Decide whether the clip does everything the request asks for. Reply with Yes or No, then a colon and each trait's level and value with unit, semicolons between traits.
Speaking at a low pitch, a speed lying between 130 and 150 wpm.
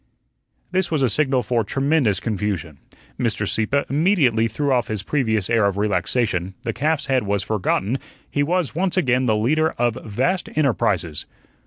No: low, 120 Hz; average, 160 wpm